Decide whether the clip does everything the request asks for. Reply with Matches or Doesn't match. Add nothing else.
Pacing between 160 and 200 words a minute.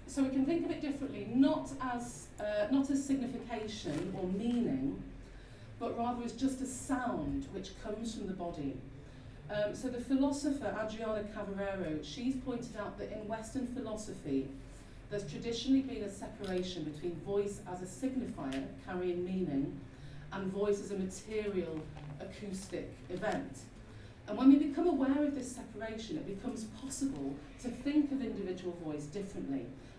Doesn't match